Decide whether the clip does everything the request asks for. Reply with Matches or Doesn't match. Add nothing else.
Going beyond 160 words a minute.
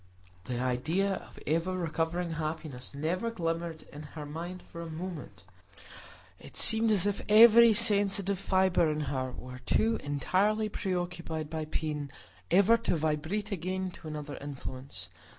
Doesn't match